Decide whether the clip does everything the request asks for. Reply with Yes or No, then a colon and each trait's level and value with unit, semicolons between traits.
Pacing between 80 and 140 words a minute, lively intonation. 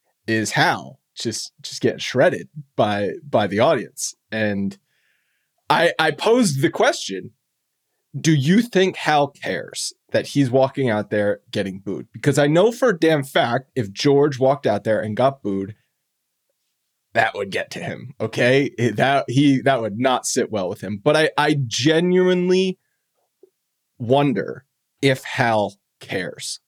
No: average, 150 wpm; wide, 6.4 semitones